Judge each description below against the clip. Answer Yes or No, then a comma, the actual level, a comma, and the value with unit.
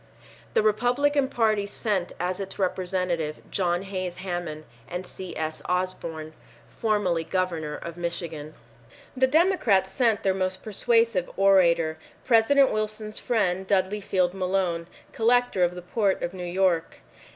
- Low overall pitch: No, medium, 185 Hz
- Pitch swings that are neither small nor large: Yes, average, 3.5 semitones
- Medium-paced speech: No, slow, 130 wpm